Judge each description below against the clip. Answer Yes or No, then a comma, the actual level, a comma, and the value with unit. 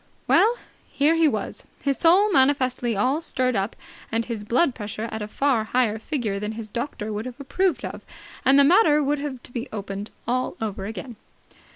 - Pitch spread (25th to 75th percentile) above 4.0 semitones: Yes, average, 4.6 semitones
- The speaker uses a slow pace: No, average, 190 wpm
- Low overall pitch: No, very high, 250 Hz